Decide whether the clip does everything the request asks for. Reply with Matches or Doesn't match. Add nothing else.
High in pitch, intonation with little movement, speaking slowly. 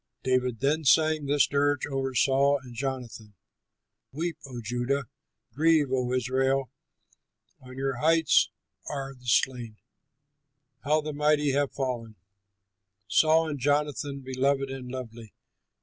Doesn't match